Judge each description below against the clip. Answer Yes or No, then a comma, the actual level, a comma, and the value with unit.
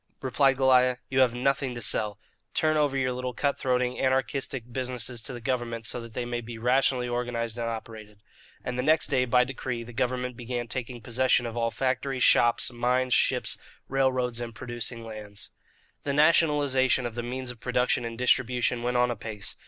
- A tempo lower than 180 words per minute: No, average, 185 wpm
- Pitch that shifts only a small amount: Yes, narrow, 1.7 semitones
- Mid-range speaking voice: No, low, 125 Hz